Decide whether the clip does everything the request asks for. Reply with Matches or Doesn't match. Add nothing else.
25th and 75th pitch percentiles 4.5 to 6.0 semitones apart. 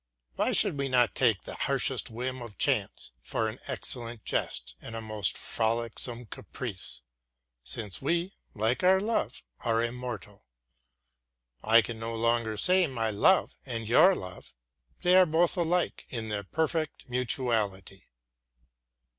Doesn't match